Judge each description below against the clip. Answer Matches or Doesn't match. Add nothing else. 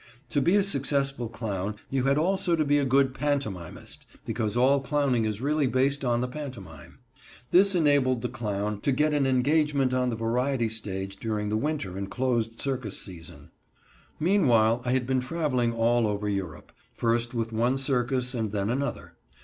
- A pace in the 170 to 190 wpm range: Matches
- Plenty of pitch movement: Doesn't match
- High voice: Doesn't match